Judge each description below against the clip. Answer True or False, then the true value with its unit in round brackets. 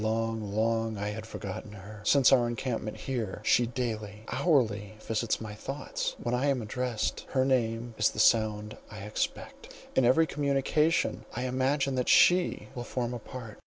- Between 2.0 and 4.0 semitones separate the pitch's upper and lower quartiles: True (3.3 semitones)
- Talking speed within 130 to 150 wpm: False (165 wpm)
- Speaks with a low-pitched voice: True (115 Hz)